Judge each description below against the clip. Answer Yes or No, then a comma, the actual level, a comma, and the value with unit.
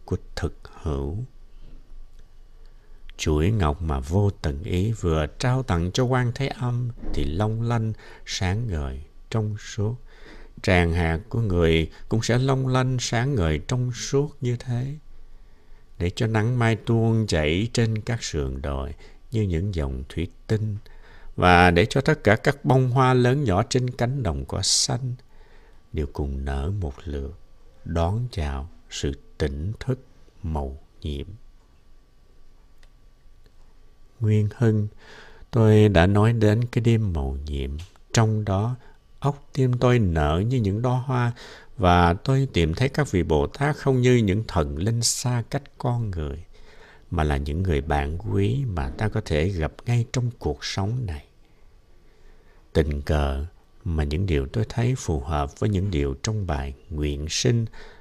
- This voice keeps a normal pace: No, slow, 155 wpm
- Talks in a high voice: No, low, 100 Hz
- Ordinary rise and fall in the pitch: No, wide, 7.4 semitones